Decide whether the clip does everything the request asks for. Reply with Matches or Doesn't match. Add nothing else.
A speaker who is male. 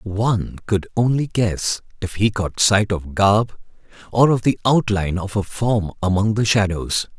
Matches